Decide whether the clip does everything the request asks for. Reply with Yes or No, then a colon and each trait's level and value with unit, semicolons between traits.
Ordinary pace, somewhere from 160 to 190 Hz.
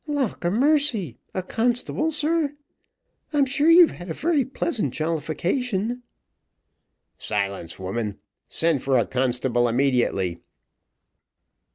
No: slow, 105 wpm; medium, 185 Hz